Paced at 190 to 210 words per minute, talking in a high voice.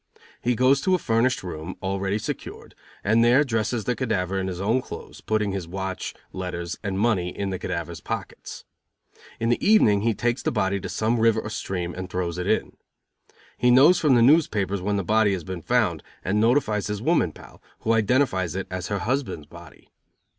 No: average, 195 wpm; low, 105 Hz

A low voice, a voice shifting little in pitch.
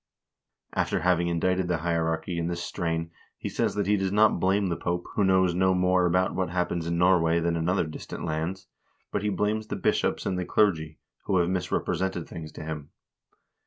Yes: very low, 90 Hz; narrow, 2.1 semitones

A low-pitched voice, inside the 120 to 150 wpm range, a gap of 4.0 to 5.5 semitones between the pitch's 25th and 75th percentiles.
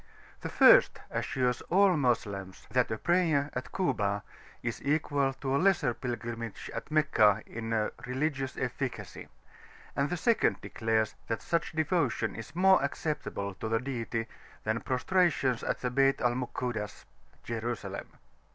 Yes: low, 125 Hz; slow, 135 wpm; average, 5.0 semitones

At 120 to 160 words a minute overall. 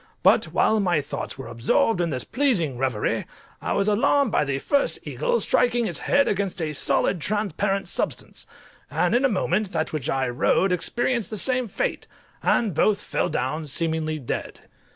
No: average, 175 wpm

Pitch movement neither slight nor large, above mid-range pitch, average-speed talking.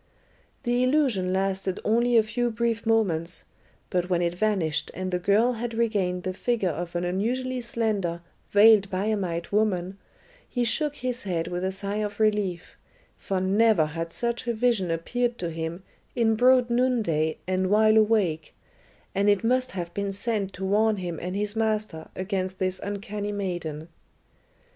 Yes: average, 3.9 semitones; high, 200 Hz; average, 160 wpm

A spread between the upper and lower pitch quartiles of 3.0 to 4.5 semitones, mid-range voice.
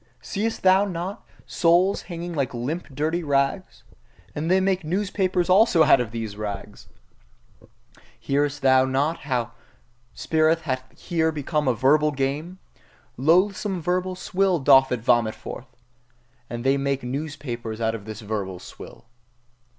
No: wide, 5.6 semitones; medium, 145 Hz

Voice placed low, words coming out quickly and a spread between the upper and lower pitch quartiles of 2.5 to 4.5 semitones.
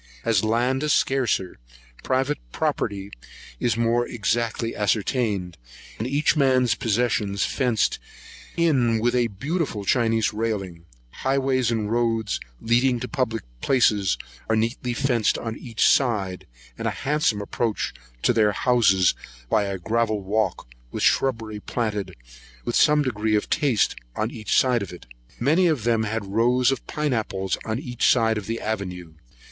No: low, 115 Hz; average, 150 wpm; average, 3.3 semitones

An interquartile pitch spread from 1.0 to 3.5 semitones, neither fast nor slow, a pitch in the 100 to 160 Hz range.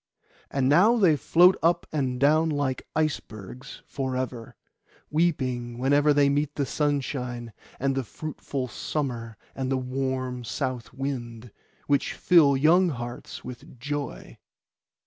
No: average, 2.9 semitones; slow, 125 wpm; low, 135 Hz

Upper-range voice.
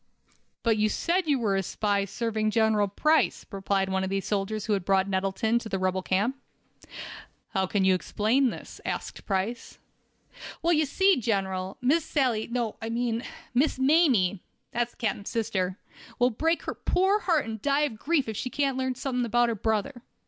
Yes: high, 225 Hz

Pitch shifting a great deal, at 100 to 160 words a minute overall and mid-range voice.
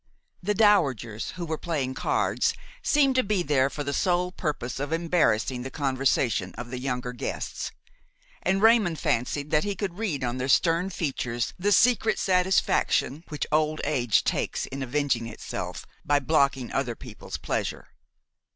Yes: wide, 6.0 semitones; average, 155 wpm; medium, 145 Hz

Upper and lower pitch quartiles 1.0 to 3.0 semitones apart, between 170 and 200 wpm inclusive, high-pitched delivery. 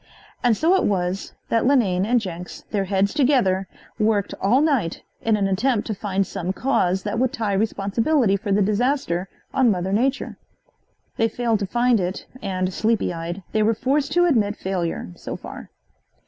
No: average, 4.3 semitones; average, 175 wpm; high, 210 Hz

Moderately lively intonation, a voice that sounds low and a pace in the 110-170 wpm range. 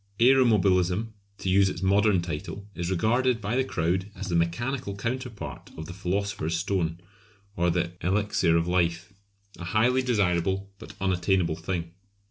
Yes: average, 3.5 semitones; very low, 95 Hz; average, 150 wpm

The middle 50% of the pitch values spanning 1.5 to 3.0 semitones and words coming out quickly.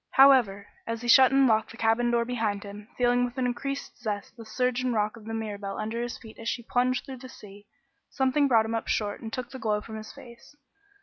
Yes: narrow, 2.6 semitones; fast, 240 wpm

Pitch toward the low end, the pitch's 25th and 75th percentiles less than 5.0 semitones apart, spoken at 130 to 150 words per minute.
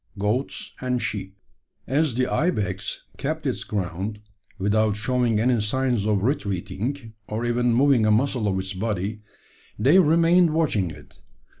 Yes: low, 110 Hz; average, 4.3 semitones; average, 140 wpm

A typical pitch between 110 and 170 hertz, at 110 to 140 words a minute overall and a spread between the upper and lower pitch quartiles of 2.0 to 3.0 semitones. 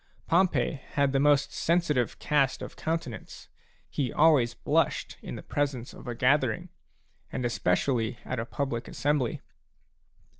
No: medium, 140 Hz; slow, 135 wpm; average, 3.4 semitones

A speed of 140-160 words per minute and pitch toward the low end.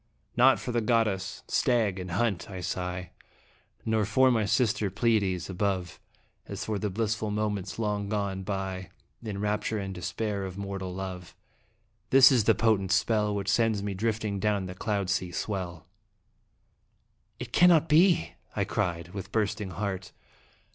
Yes: average, 150 wpm; low, 100 Hz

